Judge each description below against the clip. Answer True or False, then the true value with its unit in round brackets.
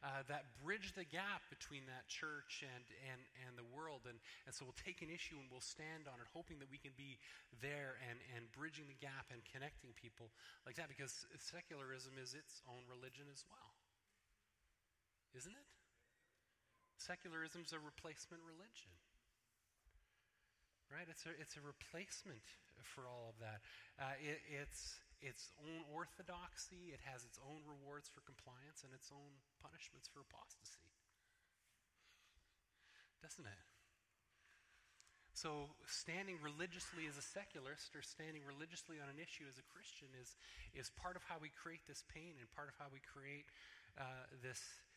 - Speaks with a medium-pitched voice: True (145 Hz)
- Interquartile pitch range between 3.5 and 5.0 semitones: True (3.8 semitones)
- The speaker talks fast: False (155 wpm)